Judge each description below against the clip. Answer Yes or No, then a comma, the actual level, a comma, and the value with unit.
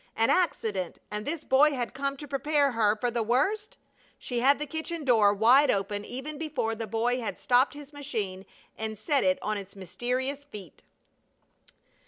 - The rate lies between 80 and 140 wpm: No, average, 175 wpm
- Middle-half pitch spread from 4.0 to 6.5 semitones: Yes, average, 4.9 semitones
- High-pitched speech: Yes, very high, 250 Hz